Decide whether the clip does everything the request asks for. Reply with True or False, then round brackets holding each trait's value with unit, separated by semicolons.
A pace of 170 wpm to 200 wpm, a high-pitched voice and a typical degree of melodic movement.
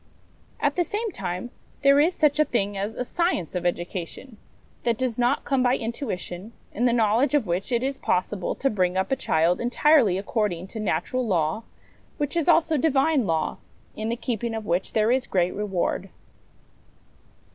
False (180 wpm; 230 Hz; 6.3 semitones)